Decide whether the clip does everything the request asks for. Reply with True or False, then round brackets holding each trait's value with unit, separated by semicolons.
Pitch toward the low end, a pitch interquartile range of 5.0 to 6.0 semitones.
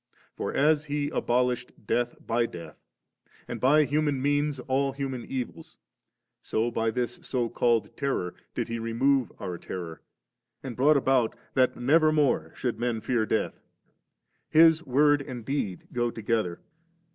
False (125 Hz; 3.6 semitones)